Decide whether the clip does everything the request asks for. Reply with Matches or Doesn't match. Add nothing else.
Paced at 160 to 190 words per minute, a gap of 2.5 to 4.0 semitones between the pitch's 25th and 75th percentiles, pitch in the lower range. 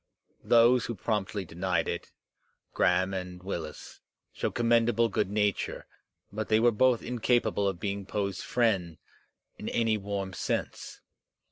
Doesn't match